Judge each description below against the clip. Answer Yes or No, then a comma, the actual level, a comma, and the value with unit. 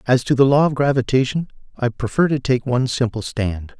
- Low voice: Yes, low, 125 Hz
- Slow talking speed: No, fast, 205 wpm